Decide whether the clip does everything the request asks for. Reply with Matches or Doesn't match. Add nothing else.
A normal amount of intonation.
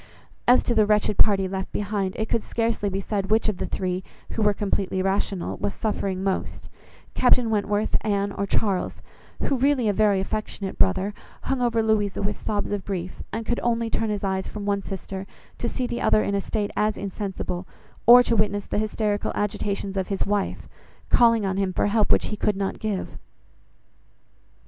Doesn't match